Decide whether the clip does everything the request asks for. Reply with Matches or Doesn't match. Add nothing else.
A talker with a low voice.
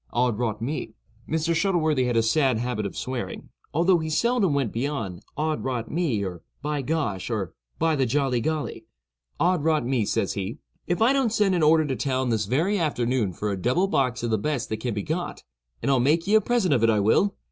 Matches